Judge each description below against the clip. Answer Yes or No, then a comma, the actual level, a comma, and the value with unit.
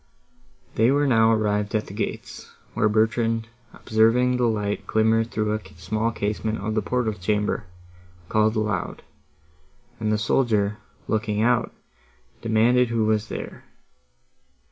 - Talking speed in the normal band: No, slow, 130 wpm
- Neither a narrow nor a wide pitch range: No, narrow, 1.3 semitones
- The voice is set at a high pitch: No, low, 110 Hz